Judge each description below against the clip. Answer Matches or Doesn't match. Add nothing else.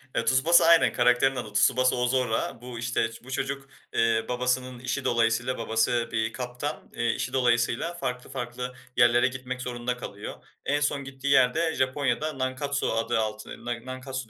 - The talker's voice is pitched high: Doesn't match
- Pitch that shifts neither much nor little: Doesn't match